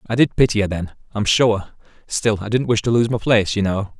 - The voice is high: No, low, 110 Hz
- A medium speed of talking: No, fast, 255 wpm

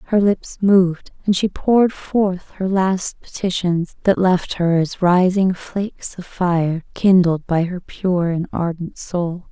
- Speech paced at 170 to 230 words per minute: No, average, 160 wpm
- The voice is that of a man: No, female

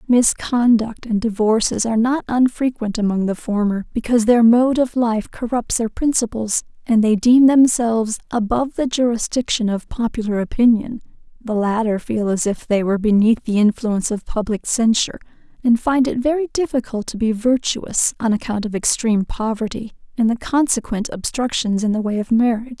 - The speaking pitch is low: No, high, 230 Hz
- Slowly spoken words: No, average, 165 wpm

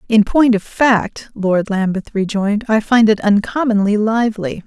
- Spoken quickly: No, average, 155 wpm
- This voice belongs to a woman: Yes, female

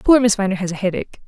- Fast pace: Yes, fast, 280 wpm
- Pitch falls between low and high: No, high, 200 Hz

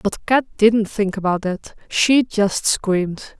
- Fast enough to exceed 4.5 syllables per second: No, 3.5 syllables/s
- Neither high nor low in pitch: No, high, 205 Hz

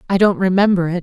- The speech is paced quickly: Yes, fast, 235 wpm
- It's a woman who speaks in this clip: Yes, female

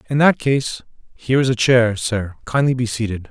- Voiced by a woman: No, male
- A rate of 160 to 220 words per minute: Yes, average, 200 wpm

